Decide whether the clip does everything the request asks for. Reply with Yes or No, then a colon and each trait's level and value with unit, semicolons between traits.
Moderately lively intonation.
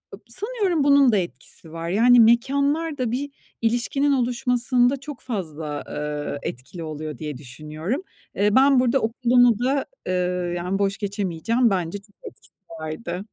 No: wide, 7.0 semitones